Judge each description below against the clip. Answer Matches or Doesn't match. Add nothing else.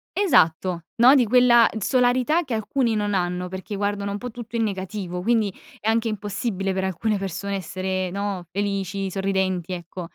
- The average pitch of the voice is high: Matches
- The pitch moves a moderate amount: Matches